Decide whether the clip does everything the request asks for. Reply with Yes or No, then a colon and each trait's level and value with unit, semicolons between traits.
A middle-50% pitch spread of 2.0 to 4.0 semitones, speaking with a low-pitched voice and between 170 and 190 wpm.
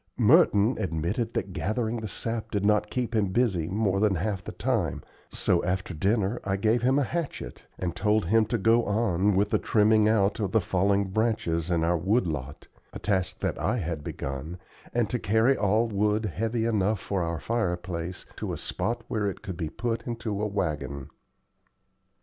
Yes: average, 3.7 semitones; low, 105 Hz; average, 185 wpm